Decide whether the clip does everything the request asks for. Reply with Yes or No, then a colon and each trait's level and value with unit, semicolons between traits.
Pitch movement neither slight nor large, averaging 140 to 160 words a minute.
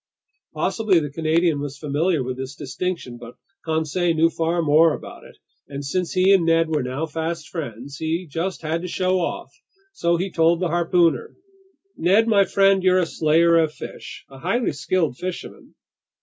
No: average, 3.4 semitones; average, 175 wpm